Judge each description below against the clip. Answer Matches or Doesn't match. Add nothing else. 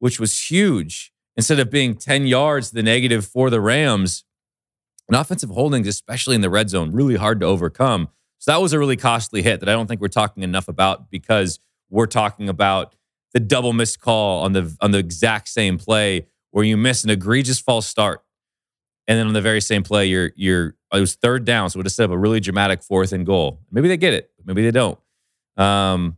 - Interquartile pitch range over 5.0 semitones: Doesn't match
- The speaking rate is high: Matches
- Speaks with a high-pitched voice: Doesn't match